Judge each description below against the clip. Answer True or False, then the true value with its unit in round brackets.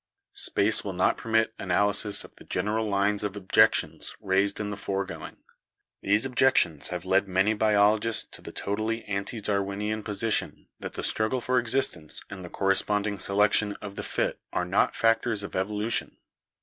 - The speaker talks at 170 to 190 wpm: False (160 wpm)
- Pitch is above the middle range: False (105 Hz)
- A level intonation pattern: True (1.7 semitones)